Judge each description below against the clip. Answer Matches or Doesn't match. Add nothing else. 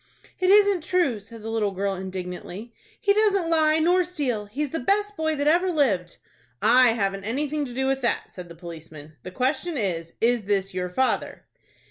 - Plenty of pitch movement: Matches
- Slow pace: Doesn't match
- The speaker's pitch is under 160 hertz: Doesn't match